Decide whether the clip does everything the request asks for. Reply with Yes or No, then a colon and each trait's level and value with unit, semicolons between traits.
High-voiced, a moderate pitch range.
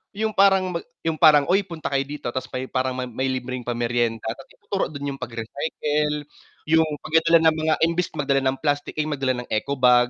No: medium, 140 Hz; average, 4.0 semitones